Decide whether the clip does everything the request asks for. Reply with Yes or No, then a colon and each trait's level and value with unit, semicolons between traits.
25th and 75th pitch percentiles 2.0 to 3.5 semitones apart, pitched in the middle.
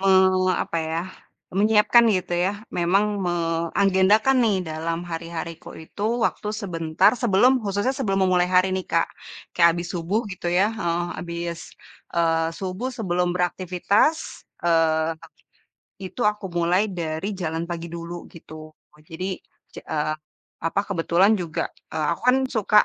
Yes: average, 3.0 semitones; medium, 175 Hz